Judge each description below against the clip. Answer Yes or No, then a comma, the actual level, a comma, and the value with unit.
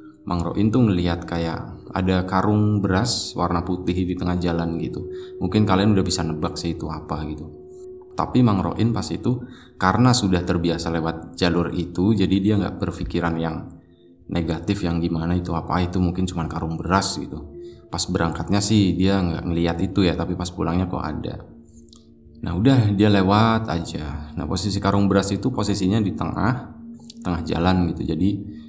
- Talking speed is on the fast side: Yes, fast, 160 wpm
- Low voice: Yes, very low, 90 Hz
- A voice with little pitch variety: No, average, 3.4 semitones